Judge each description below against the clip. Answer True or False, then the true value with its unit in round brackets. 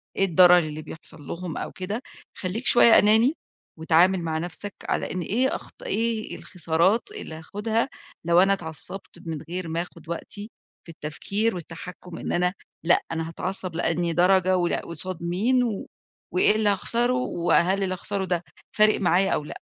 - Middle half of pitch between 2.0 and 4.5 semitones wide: True (3.5 semitones)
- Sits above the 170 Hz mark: True (185 Hz)